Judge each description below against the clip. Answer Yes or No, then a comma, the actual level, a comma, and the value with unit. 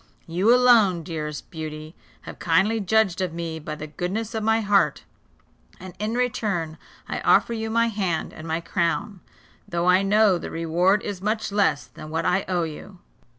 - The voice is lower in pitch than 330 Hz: Yes, medium, 185 Hz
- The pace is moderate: Yes, average, 175 wpm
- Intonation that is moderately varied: Yes, average, 4.6 semitones